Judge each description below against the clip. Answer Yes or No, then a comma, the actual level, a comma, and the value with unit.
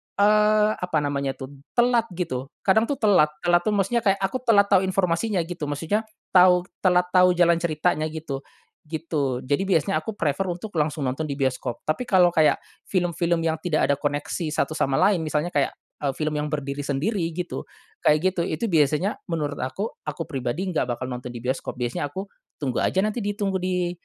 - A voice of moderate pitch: Yes, medium, 170 Hz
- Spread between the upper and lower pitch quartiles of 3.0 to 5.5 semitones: Yes, average, 4.8 semitones